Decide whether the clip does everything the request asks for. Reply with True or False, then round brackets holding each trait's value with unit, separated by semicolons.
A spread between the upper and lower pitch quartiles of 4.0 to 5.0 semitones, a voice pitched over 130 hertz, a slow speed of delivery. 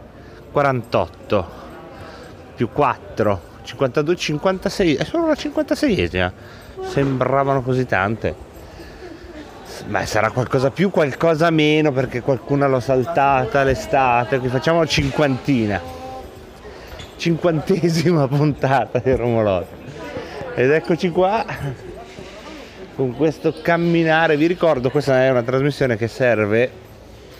True (4.6 semitones; 140 Hz; 95 wpm)